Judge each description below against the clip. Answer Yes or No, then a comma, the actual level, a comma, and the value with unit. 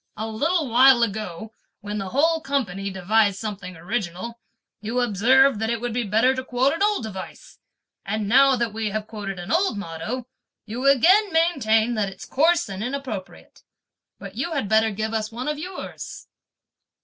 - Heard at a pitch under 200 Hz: No, high, 225 Hz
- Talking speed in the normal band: Yes, average, 175 wpm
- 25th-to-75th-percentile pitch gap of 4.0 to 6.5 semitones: Yes, average, 4.5 semitones